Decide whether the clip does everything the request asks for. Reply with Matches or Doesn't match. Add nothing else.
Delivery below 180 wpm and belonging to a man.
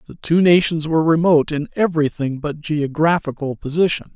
Matches